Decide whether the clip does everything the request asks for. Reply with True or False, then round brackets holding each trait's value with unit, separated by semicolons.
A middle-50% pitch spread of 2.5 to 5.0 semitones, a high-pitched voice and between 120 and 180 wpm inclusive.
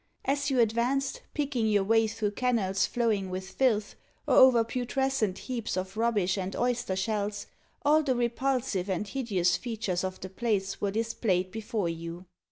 True (4.5 semitones; 220 Hz; 160 wpm)